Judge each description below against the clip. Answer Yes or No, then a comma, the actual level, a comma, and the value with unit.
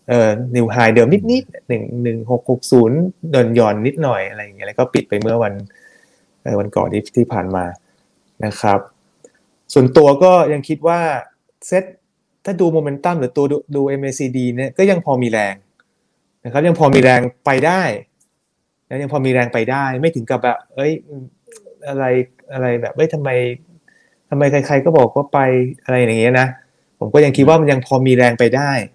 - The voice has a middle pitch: No, low, 130 Hz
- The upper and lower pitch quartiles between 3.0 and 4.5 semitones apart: Yes, average, 3.7 semitones